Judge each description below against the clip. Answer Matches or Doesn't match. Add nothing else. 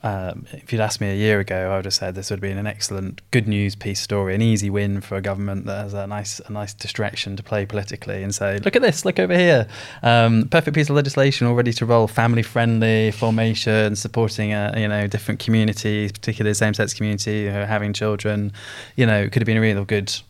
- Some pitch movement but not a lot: Doesn't match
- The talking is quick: Matches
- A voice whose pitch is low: Matches